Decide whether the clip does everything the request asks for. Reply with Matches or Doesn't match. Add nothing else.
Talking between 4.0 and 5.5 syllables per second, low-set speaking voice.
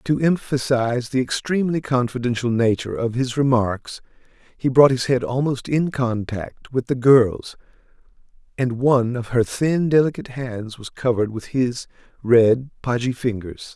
Matches